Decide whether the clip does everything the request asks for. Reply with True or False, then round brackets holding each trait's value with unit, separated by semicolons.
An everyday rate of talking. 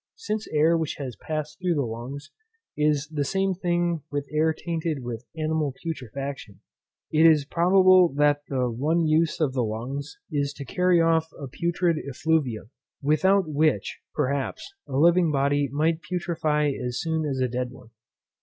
True (155 wpm)